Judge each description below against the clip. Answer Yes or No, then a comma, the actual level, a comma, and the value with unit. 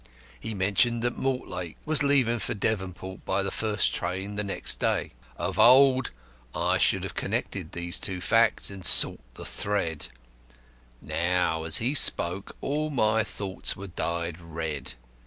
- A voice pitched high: No, low, 100 Hz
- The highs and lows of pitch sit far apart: No, average, 4.7 semitones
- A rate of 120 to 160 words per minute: Yes, average, 155 wpm